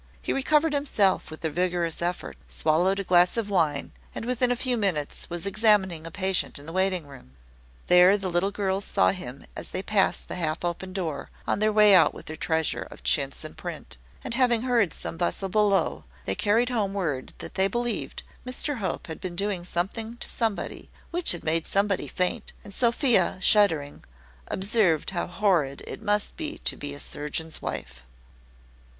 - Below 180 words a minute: No, average, 185 wpm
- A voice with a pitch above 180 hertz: Yes, high, 190 Hz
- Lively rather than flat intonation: No, average, 4.5 semitones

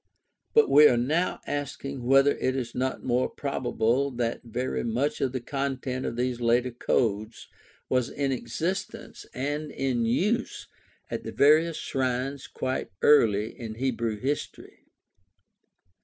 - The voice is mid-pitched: No, low, 130 Hz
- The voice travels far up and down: No, average, 2.8 semitones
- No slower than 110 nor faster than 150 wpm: Yes, slow, 135 wpm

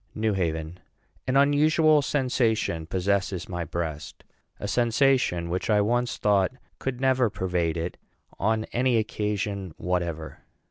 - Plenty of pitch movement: Yes, wide, 5.9 semitones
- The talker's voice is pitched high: No, low, 105 Hz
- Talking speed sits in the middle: No, slow, 125 wpm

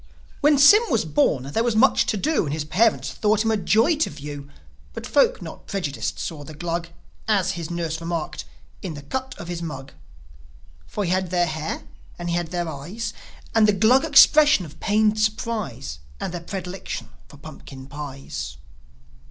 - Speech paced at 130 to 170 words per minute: No, average, 180 wpm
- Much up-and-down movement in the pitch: Yes, wide, 6.3 semitones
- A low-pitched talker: No, medium, 175 Hz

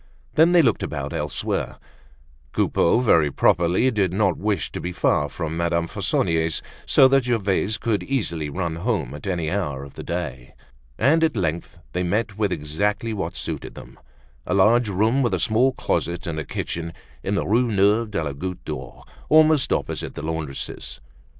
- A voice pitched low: Yes, very low, 95 Hz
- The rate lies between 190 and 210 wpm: No, average, 175 wpm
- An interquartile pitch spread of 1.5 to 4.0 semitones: No, wide, 5.6 semitones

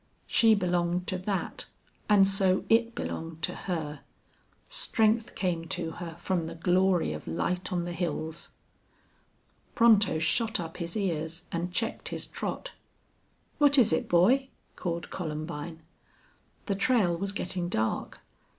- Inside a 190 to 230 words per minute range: No, slow, 135 wpm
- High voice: No, medium, 180 Hz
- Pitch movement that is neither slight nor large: Yes, average, 3.3 semitones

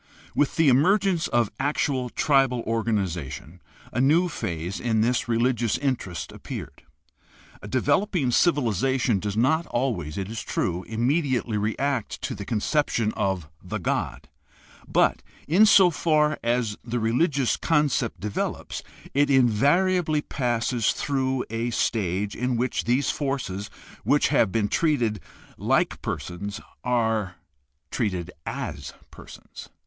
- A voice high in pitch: No, low, 120 Hz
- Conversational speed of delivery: No, slow, 125 wpm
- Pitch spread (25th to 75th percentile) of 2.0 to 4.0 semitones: No, average, 5.0 semitones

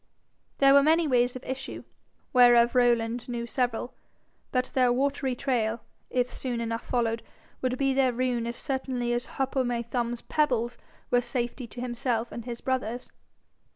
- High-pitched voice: Yes, high, 245 Hz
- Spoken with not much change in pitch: Yes, narrow, 1.6 semitones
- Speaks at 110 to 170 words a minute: Yes, average, 160 wpm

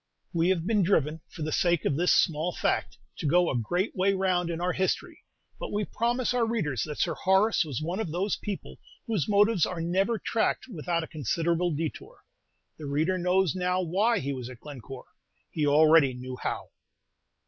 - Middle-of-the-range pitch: Yes, medium, 175 Hz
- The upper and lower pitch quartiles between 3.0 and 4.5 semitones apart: Yes, average, 3.9 semitones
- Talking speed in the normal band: Yes, average, 190 wpm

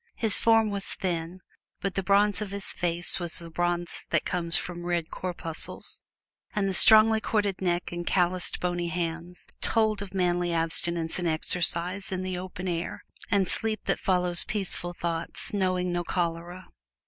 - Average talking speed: Yes, average, 160 wpm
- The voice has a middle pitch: Yes, medium, 180 Hz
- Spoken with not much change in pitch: Yes, narrow, 2.1 semitones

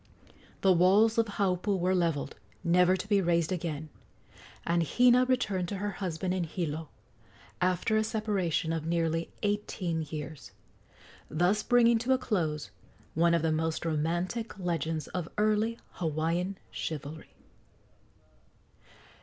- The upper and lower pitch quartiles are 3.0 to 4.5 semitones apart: Yes, average, 4.1 semitones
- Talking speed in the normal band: No, slow, 130 wpm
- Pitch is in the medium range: Yes, medium, 180 Hz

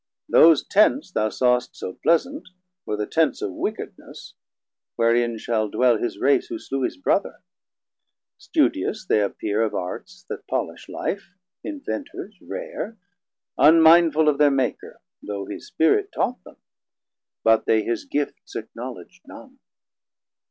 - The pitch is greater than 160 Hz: No, medium, 140 Hz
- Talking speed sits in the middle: No, slow, 130 wpm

